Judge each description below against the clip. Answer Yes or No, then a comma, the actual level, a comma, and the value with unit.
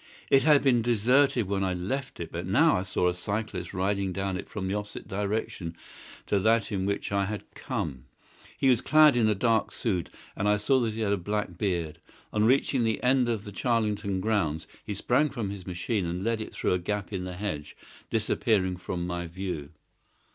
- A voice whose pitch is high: No, low, 100 Hz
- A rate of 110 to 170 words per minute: No, fast, 205 wpm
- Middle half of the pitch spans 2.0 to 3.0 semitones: No, average, 3.7 semitones